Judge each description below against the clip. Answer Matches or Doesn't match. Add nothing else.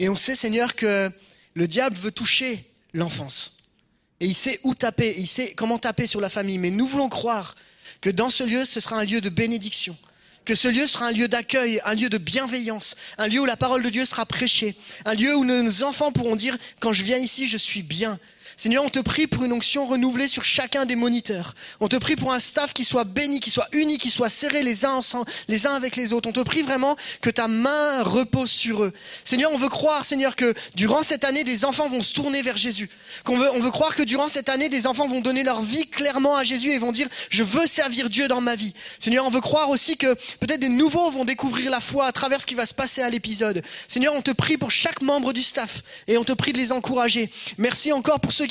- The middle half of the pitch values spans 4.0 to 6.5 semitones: Doesn't match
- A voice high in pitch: Matches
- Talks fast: Matches